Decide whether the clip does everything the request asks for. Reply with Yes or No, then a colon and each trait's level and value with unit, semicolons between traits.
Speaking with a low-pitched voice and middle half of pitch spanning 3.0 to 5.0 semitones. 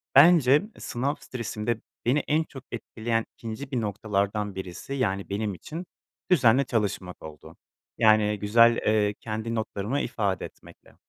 Yes: low, 110 Hz; average, 3.7 semitones